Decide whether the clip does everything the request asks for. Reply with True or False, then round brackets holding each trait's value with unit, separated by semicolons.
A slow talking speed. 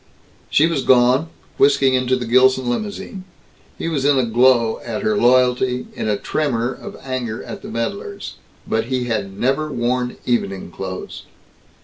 False (155 wpm)